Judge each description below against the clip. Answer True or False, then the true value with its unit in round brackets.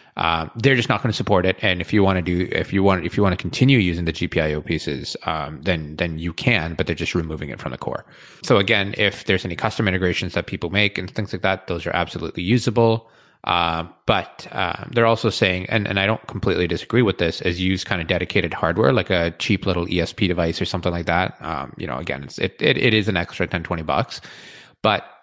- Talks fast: True (245 wpm)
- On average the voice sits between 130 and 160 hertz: False (95 Hz)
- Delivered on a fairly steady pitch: False (3.4 semitones)